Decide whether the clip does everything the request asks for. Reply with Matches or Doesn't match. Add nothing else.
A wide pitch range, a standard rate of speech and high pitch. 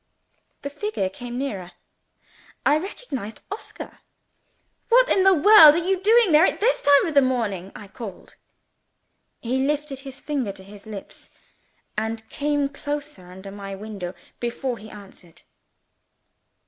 Matches